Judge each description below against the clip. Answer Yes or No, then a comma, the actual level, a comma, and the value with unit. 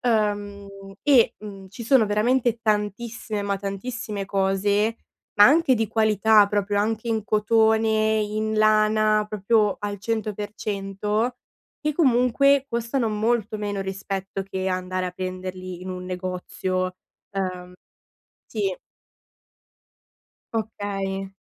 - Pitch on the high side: Yes, high, 210 Hz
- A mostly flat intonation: Yes, narrow, 2.3 semitones